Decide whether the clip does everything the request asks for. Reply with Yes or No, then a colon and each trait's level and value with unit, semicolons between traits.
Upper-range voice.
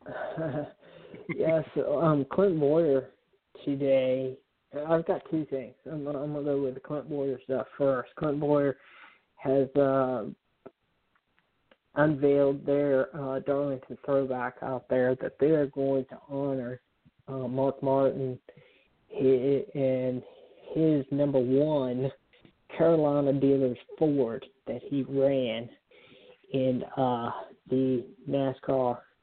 No: low, 135 Hz